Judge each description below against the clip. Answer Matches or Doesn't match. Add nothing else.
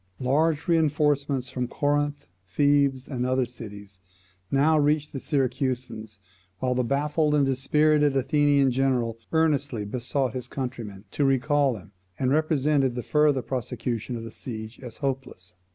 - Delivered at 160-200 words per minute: Doesn't match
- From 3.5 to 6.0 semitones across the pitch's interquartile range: Doesn't match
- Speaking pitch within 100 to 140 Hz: Matches